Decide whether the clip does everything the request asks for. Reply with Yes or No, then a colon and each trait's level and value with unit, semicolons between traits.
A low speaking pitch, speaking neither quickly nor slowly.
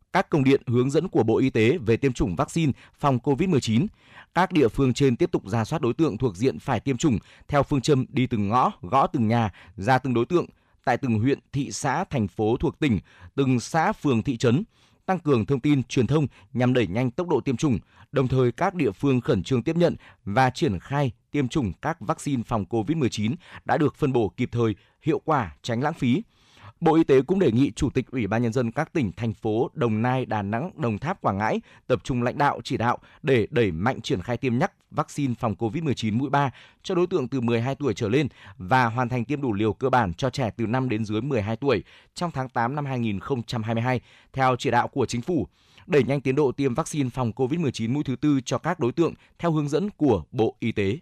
Yes: low, 130 Hz; average, 235 wpm